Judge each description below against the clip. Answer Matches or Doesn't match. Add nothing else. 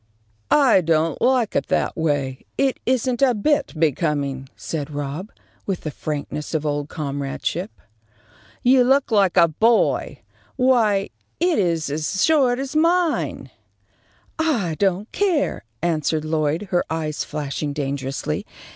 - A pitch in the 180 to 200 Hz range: Doesn't match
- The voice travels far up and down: Matches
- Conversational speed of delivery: Doesn't match